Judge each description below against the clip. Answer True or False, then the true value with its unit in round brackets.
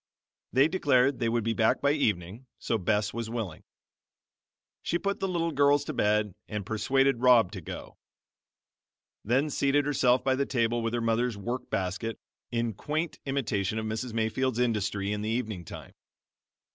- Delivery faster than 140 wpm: True (165 wpm)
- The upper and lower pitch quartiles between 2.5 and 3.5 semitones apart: False (3.9 semitones)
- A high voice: False (115 Hz)